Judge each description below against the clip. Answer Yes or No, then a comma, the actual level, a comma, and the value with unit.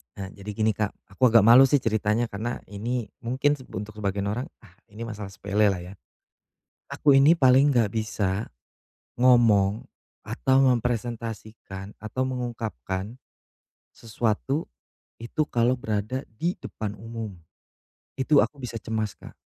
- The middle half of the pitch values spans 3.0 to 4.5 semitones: Yes, average, 3.3 semitones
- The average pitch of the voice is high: No, low, 115 Hz